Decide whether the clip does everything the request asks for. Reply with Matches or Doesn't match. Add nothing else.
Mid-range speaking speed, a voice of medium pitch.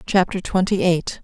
Matches